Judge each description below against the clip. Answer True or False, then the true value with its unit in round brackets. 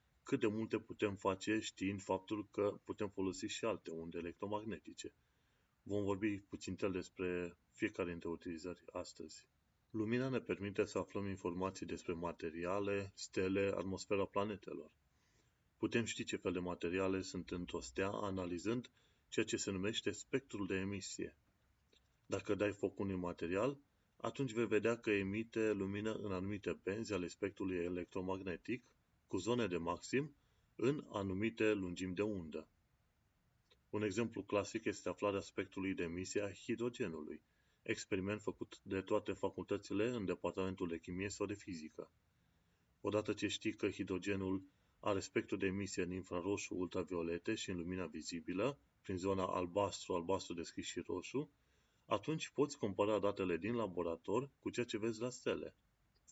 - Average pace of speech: True (145 wpm)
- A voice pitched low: True (100 Hz)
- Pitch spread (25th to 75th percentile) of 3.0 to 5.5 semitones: False (2.5 semitones)